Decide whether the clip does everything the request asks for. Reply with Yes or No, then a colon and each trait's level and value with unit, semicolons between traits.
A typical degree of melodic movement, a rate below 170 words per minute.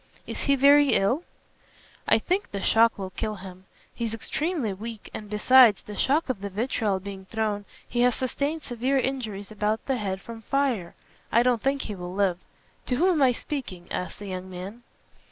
No: average, 4.9 semitones; average, 190 wpm